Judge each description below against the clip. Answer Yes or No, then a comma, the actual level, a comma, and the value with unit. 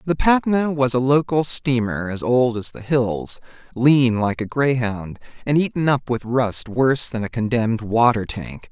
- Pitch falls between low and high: No, low, 125 Hz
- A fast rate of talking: No, average, 180 wpm